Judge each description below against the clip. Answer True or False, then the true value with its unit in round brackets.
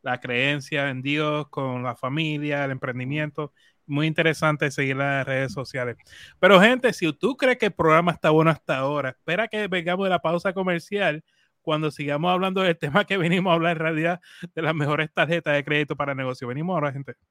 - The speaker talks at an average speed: False (200 wpm)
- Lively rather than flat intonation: False (3.6 semitones)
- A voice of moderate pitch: True (155 Hz)